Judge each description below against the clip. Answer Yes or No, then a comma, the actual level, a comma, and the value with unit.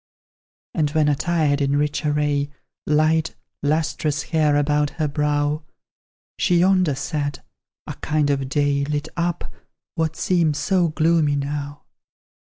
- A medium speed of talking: No, slow, 125 wpm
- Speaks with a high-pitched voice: No, medium, 150 Hz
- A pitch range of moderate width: No, narrow, 1.7 semitones